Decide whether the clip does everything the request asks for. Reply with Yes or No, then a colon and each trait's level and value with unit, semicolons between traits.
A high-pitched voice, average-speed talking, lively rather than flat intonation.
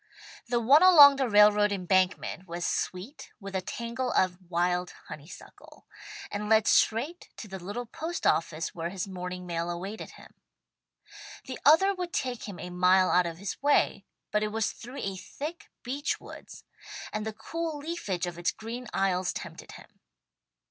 Yes: high, 205 Hz; average, 165 wpm; wide, 5.8 semitones